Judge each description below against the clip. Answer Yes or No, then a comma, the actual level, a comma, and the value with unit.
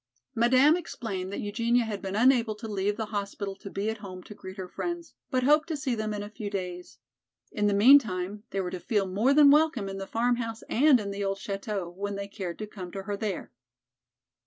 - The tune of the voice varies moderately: Yes, average, 3.4 semitones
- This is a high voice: Yes, high, 210 Hz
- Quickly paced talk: Yes, fast, 225 wpm